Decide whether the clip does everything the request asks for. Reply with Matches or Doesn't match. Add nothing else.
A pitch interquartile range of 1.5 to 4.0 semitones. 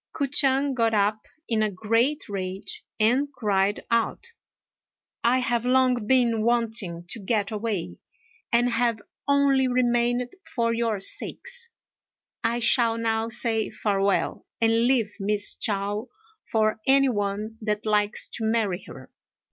Matches